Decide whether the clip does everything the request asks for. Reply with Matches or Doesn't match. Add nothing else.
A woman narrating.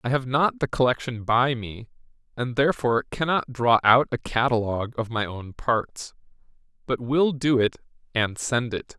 Doesn't match